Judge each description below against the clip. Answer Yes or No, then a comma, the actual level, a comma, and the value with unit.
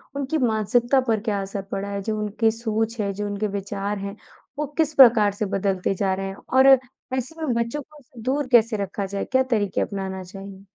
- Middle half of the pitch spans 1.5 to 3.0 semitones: No, average, 3.5 semitones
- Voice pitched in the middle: No, high, 210 Hz